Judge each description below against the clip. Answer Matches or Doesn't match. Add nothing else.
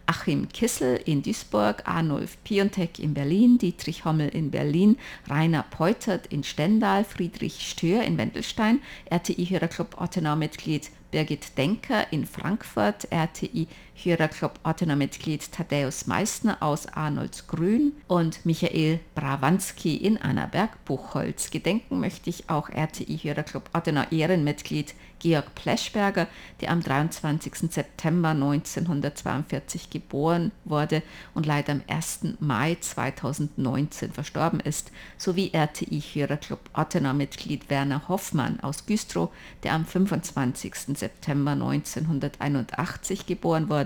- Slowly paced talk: Matches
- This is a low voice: Doesn't match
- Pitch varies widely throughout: Doesn't match